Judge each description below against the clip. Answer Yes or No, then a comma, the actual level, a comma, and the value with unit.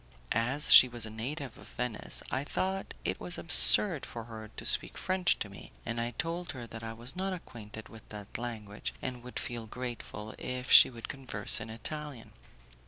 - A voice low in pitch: Yes, low, 120 Hz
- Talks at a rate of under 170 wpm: No, average, 190 wpm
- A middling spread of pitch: Yes, average, 3.6 semitones